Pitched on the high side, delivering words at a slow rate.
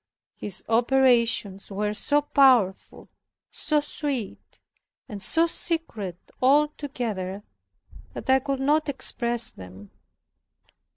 Yes: high, 245 Hz; slow, 100 wpm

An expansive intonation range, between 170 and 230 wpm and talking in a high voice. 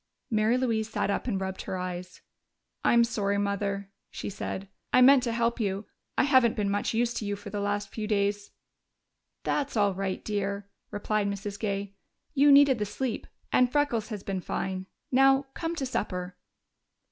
No: average, 3.1 semitones; average, 175 wpm; high, 210 Hz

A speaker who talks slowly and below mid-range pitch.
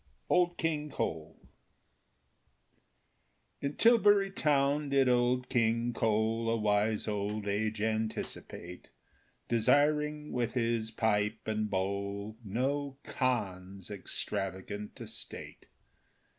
Yes: slow, 90 wpm; low, 110 Hz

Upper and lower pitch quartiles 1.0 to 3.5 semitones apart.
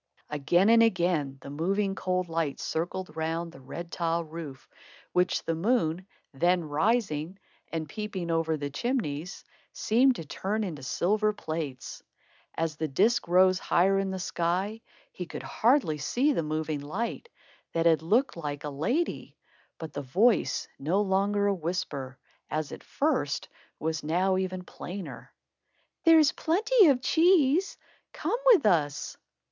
No: average, 5.1 semitones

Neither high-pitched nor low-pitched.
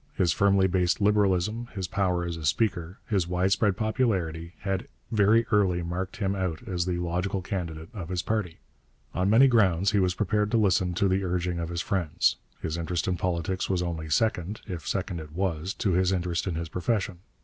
No: very low, 90 Hz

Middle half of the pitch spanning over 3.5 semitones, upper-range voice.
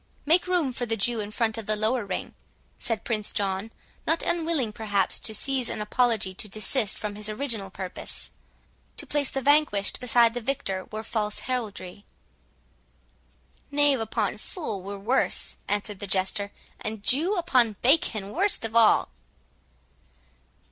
Yes: average, 4.2 semitones; high, 220 Hz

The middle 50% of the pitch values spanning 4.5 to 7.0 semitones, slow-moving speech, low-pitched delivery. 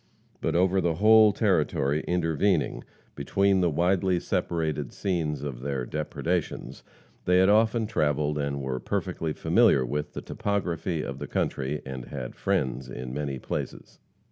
No: average, 4.9 semitones; average, 145 wpm; very low, 80 Hz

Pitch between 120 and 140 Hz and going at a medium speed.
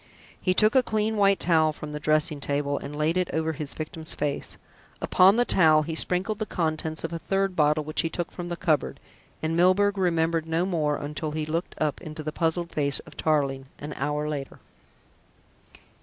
No: medium, 160 Hz; average, 195 wpm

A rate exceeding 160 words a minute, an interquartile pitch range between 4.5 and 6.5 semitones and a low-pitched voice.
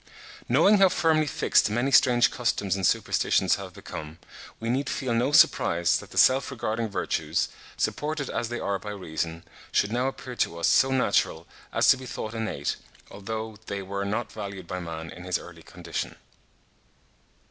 Yes: average, 170 wpm; average, 5.2 semitones; low, 110 Hz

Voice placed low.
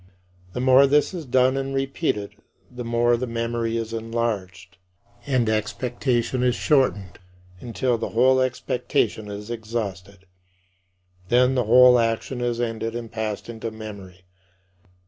Yes: low, 115 Hz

